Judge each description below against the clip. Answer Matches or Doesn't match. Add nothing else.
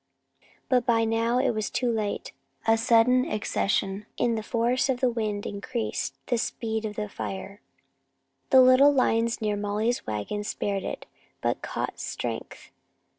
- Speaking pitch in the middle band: Doesn't match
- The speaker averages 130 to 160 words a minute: Matches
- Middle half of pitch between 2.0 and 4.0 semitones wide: Matches